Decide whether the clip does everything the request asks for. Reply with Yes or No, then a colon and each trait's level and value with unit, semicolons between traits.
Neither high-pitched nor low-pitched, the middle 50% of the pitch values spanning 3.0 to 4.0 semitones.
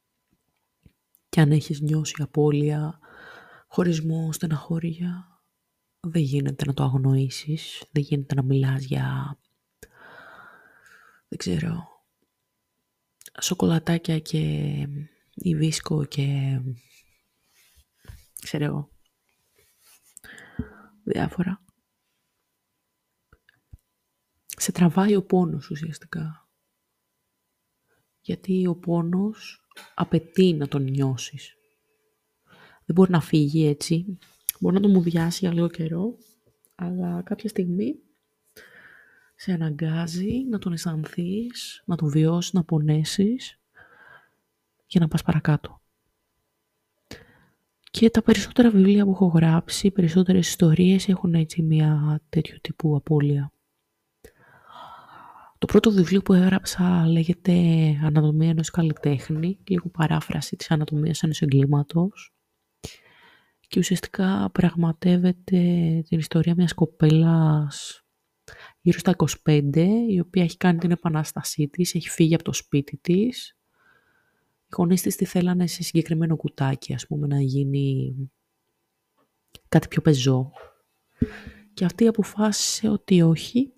Yes: medium, 165 Hz; average, 3.4 semitones